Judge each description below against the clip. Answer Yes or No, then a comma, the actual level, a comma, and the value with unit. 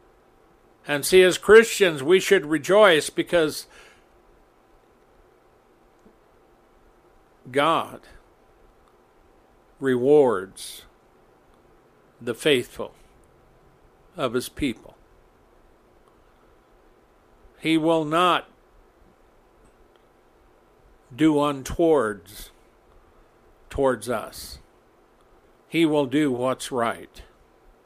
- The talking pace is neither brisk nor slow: No, slow, 60 wpm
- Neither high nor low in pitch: Yes, medium, 155 Hz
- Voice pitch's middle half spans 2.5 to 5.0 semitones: No, wide, 5.4 semitones